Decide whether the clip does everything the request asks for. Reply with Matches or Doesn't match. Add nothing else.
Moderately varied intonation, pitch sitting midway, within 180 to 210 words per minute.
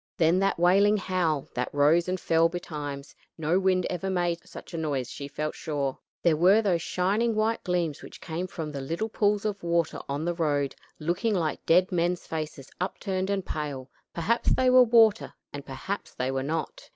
Matches